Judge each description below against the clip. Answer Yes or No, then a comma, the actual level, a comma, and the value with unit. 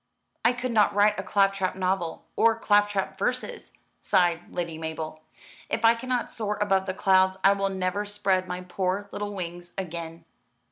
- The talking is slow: No, average, 160 wpm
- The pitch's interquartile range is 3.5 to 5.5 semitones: No, narrow, 2.4 semitones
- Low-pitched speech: No, high, 195 Hz